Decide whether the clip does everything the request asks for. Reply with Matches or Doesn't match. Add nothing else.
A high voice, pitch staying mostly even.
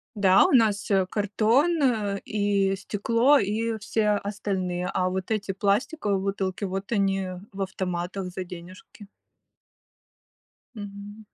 Matches